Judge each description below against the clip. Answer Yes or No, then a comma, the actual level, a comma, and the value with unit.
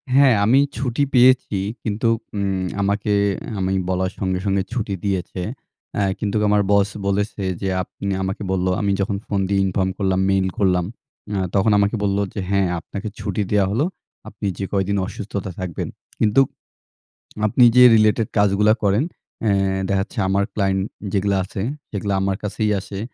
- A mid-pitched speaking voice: No, low, 100 Hz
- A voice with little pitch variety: Yes, narrow, 1.6 semitones